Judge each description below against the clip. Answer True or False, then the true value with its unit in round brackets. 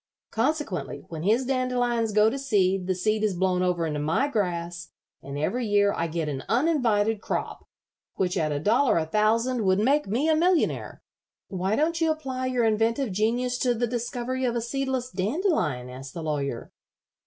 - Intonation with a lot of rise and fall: True (6.0 semitones)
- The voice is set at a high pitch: True (220 Hz)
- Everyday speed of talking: True (175 wpm)